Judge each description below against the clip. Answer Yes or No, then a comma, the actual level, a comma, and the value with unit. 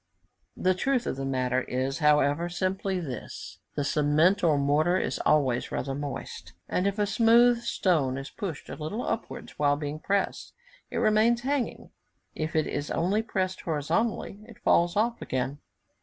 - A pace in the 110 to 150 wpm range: No, average, 160 wpm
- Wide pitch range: Yes, wide, 6.2 semitones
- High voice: No, medium, 170 Hz